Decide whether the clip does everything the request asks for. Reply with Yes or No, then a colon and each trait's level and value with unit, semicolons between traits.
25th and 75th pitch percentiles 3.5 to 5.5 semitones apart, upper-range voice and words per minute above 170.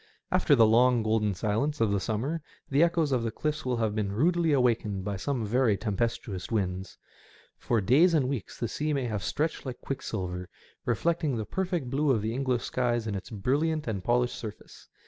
No: average, 4.9 semitones; low, 120 Hz; average, 190 wpm